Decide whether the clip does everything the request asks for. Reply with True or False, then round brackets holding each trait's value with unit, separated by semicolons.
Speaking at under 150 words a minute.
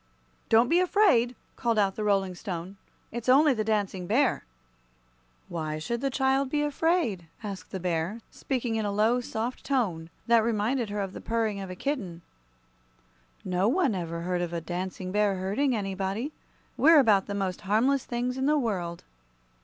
False (170 wpm)